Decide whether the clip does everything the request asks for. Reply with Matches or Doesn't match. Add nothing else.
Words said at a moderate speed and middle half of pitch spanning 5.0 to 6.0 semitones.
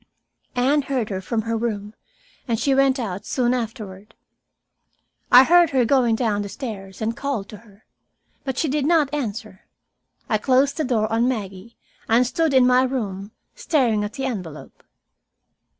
Doesn't match